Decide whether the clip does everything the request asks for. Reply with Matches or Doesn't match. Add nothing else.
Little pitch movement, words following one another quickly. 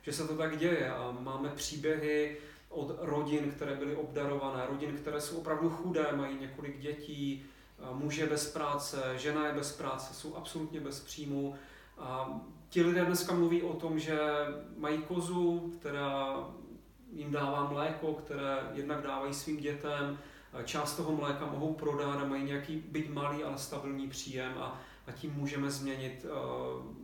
Doesn't match